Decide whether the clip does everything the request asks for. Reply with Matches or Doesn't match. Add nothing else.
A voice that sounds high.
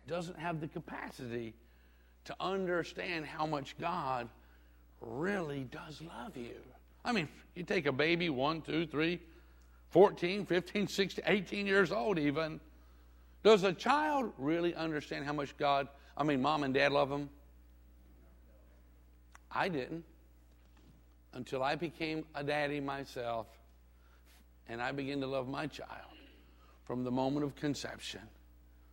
Doesn't match